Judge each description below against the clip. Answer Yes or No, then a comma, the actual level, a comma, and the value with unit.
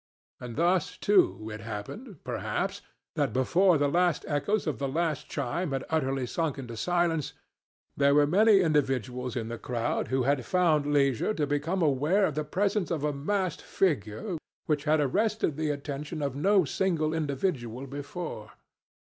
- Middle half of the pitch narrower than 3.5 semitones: No, average, 4.8 semitones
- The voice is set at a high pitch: No, medium, 150 Hz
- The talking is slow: No, average, 160 wpm